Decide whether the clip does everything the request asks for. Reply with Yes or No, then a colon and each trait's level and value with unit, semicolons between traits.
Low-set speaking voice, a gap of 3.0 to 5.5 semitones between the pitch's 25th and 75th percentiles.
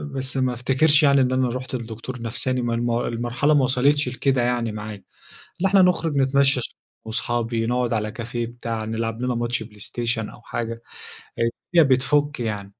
No: low, 120 Hz; narrow, 2.5 semitones